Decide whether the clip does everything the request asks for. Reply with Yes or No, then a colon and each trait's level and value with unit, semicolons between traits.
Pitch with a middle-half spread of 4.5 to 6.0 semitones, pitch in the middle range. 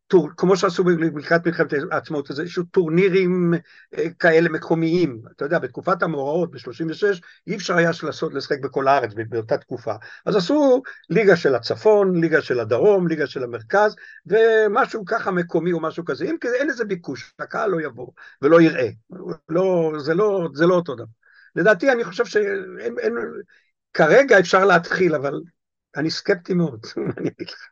Yes: average, 4.8 semitones; medium, 175 Hz